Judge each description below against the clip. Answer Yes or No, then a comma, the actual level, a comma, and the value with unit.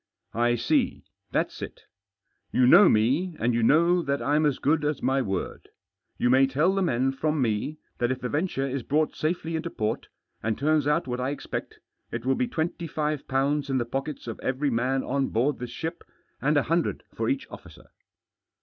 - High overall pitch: No, medium, 140 Hz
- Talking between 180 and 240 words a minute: Yes, average, 200 wpm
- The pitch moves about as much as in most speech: Yes, average, 3.7 semitones